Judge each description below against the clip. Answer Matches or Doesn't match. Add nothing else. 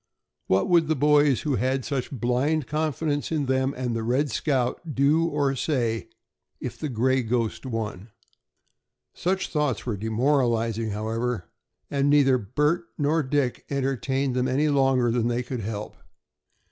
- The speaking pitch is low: Matches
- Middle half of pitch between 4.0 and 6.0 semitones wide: Doesn't match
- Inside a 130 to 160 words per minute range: Matches